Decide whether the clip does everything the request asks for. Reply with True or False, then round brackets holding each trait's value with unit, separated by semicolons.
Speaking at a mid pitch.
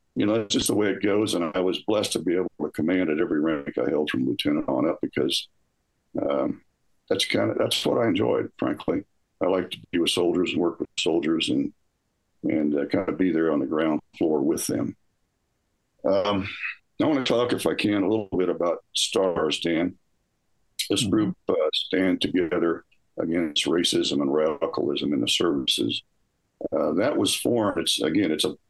False (330 Hz)